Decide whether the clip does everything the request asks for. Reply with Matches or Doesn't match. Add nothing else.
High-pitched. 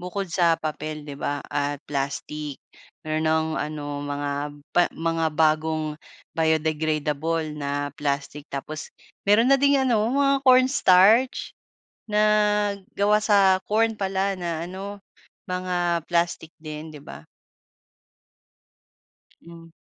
Doesn't match